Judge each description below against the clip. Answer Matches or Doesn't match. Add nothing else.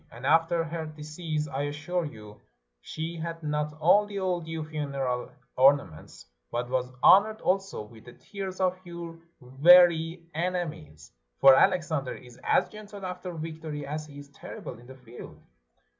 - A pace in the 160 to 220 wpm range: Doesn't match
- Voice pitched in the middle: Matches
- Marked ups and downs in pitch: Doesn't match